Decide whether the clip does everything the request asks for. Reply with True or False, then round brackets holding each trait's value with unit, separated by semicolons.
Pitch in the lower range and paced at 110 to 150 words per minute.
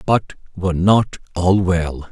True (90 Hz; 140 wpm)